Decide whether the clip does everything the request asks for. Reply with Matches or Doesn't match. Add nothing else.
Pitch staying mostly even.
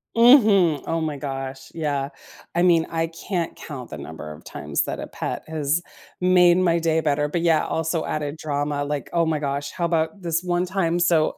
Doesn't match